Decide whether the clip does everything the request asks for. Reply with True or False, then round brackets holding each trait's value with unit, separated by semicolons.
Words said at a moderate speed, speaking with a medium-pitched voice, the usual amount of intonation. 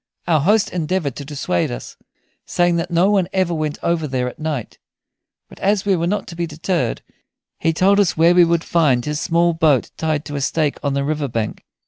False (210 wpm; 165 Hz; 3.2 semitones)